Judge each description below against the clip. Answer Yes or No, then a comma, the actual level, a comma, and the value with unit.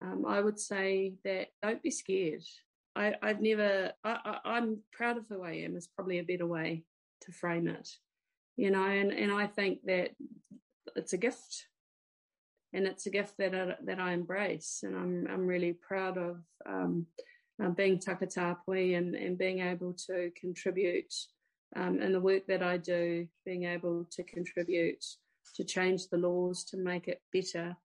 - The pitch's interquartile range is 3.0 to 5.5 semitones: No, narrow, 2.6 semitones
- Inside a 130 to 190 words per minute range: Yes, average, 175 wpm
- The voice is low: No, medium, 185 Hz